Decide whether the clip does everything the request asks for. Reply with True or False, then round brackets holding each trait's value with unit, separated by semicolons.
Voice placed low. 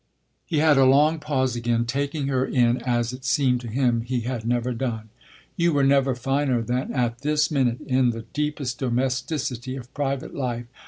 True (130 Hz)